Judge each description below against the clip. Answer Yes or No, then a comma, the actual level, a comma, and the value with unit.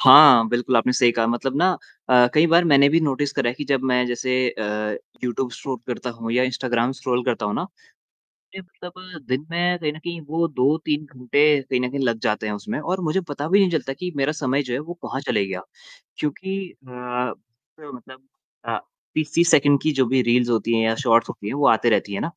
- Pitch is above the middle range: No, low, 135 Hz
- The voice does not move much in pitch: No, average, 4.1 semitones